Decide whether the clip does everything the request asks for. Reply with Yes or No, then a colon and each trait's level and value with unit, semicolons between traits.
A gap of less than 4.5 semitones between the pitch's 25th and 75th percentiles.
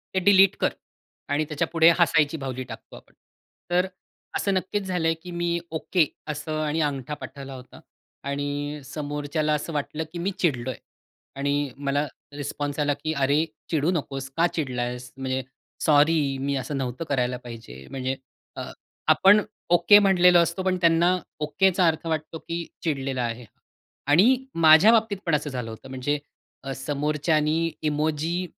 Yes: average, 3.7 semitones